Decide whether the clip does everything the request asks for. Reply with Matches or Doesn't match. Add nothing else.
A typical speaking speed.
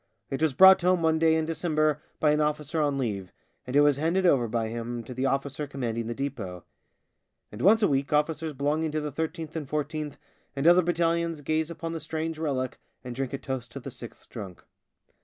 Doesn't match